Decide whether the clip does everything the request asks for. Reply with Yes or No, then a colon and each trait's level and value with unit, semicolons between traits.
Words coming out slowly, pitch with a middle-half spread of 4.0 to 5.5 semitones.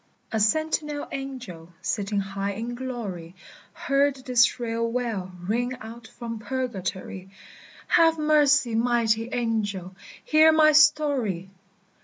Yes: slow, 110 wpm; average, 5.1 semitones